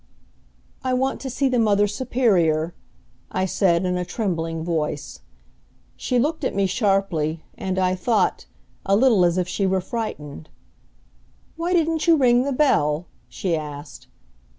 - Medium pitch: No, high, 195 Hz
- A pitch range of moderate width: No, wide, 6.8 semitones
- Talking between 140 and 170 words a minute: Yes, average, 150 wpm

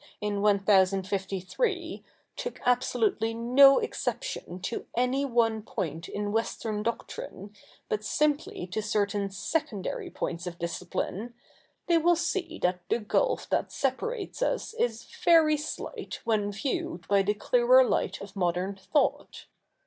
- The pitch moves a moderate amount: No, wide, 8.5 semitones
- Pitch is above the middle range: Yes, high, 225 Hz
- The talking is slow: Yes, slow, 125 wpm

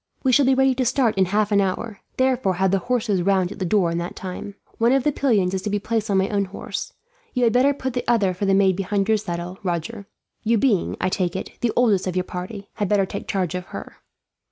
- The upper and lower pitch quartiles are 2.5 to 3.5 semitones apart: No, average, 3.9 semitones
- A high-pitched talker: Yes, high, 200 Hz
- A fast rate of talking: Yes, fast, 255 wpm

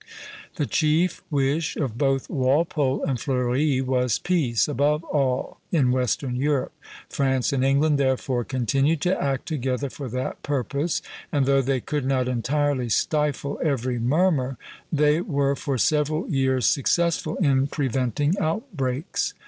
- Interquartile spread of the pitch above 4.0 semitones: No, average, 2.7 semitones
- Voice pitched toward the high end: No, medium, 140 Hz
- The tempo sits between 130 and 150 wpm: Yes, slow, 135 wpm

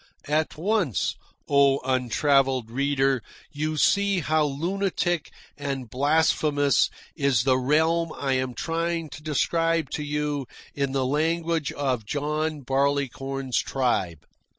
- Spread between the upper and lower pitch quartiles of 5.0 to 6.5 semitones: No, average, 3.0 semitones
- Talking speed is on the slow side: Yes, slow, 115 wpm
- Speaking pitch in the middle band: Yes, medium, 145 Hz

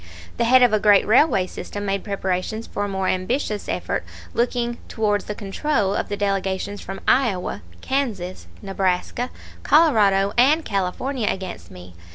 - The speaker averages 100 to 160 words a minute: Yes, average, 150 wpm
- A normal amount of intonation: Yes, average, 3.8 semitones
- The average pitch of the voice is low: No, high, 205 Hz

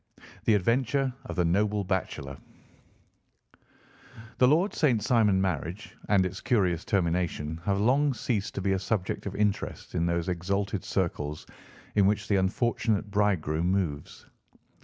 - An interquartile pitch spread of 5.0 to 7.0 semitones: No, average, 3.4 semitones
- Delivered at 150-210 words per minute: No, average, 140 wpm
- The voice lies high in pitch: No, low, 100 Hz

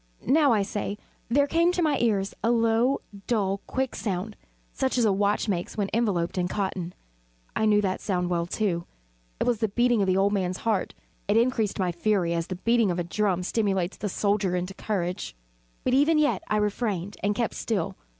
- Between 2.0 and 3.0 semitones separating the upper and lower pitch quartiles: No, average, 3.8 semitones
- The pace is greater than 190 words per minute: Yes, average, 200 wpm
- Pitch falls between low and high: No, high, 205 Hz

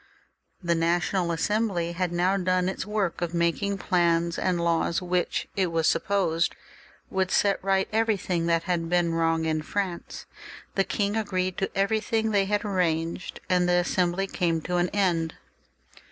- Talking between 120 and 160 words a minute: Yes, average, 155 wpm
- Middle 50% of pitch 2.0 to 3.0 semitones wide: Yes, narrow, 2.4 semitones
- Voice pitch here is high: No, medium, 180 Hz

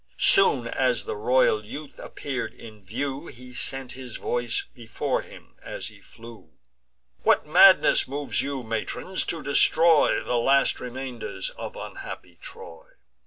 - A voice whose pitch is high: No, low, 135 Hz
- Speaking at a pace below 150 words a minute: Yes, slow, 135 wpm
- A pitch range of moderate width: Yes, average, 4.5 semitones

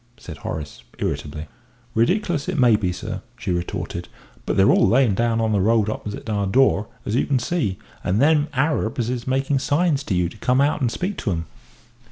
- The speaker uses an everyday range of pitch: No, wide, 5.7 semitones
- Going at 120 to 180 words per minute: No, average, 200 wpm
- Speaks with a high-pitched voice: No, low, 115 Hz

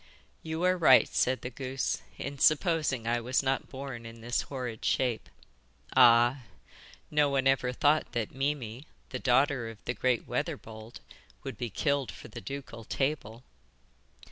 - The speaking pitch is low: Yes, low, 130 Hz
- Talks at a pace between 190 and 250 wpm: No, average, 150 wpm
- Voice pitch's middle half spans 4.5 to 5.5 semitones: No, average, 3.0 semitones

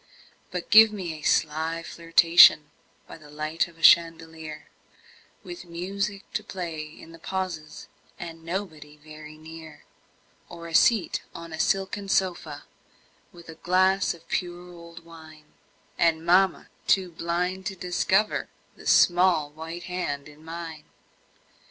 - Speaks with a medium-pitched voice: Yes, medium, 170 Hz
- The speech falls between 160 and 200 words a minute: No, slow, 135 wpm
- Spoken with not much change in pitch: Yes, narrow, 2.3 semitones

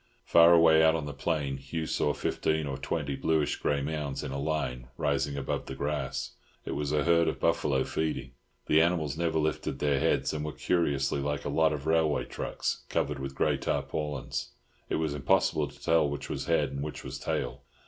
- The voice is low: Yes, very low, 75 Hz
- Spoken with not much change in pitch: Yes, narrow, 2.3 semitones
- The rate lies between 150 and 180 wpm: No, average, 200 wpm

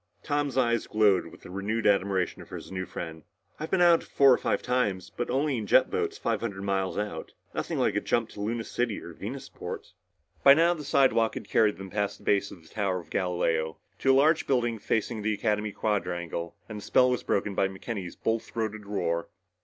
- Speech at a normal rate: No, fast, 210 wpm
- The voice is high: No, low, 105 Hz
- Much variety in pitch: No, average, 4.2 semitones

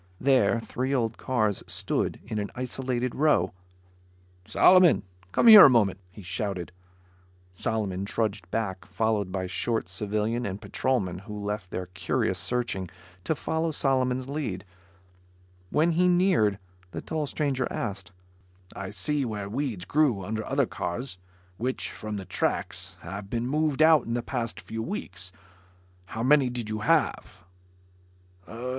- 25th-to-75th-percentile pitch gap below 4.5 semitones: No, average, 5.2 semitones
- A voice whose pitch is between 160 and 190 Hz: No, low, 115 Hz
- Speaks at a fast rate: No, average, 140 wpm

